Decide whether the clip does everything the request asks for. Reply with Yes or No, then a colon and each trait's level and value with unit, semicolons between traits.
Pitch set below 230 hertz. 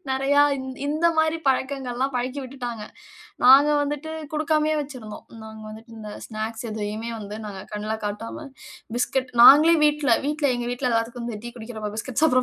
No: very high, 250 Hz